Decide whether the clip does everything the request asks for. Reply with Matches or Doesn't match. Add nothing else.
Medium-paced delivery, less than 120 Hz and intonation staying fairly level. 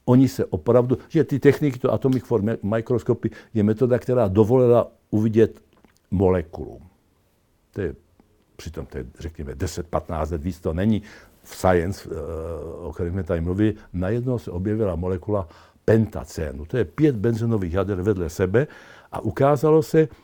Doesn't match